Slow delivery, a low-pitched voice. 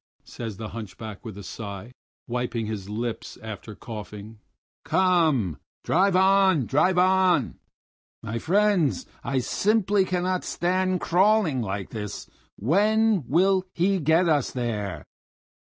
No: slow, 120 wpm; medium, 150 Hz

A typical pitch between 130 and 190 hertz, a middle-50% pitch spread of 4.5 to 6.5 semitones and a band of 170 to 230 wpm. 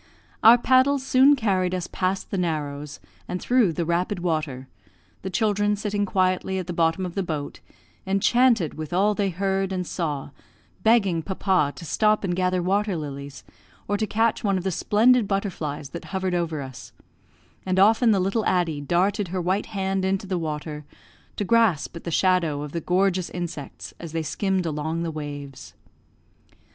No: medium, 185 Hz; average, 3.6 semitones; average, 175 wpm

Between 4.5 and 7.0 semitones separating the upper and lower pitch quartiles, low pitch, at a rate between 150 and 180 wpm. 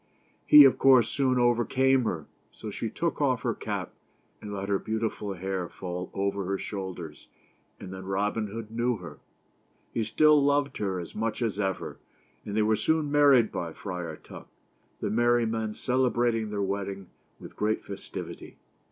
No: average, 3.8 semitones; low, 105 Hz; average, 175 wpm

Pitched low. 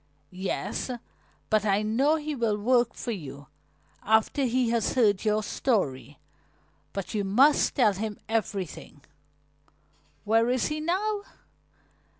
No: high, 220 Hz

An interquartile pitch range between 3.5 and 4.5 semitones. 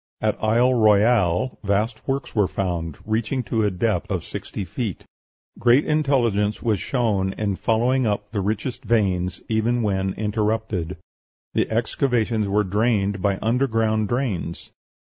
No: average, 3.0 semitones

